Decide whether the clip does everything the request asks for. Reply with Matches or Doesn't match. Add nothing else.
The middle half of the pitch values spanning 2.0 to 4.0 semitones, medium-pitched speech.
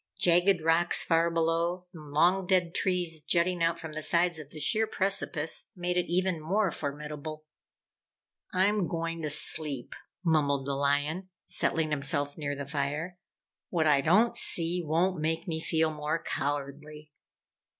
Matches